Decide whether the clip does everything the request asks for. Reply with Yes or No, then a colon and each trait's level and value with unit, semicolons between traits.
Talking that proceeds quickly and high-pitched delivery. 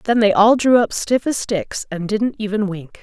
Yes: fast, 240 wpm; high, 210 Hz